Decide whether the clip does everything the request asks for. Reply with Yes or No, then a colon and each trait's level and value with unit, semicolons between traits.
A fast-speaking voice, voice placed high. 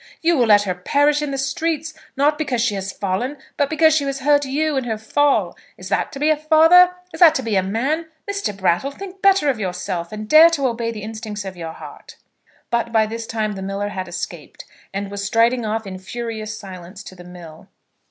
Yes: fast, 220 wpm; high, 230 Hz